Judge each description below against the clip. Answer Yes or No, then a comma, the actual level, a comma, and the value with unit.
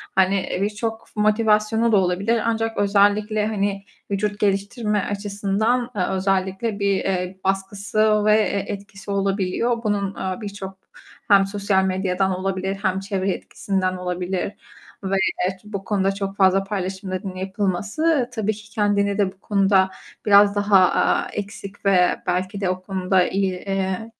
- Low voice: No, high, 200 Hz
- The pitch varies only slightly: Yes, narrow, 1.6 semitones